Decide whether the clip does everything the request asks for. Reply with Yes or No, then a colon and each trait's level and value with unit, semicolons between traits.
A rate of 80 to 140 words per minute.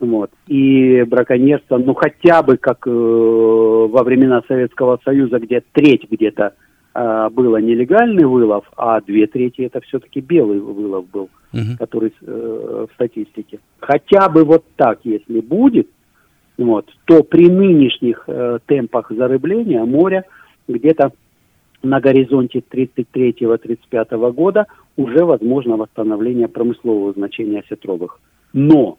Yes: average, 120 wpm